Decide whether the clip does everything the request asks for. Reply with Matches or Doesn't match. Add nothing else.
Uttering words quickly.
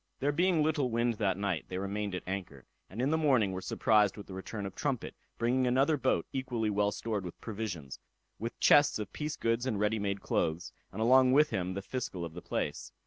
Matches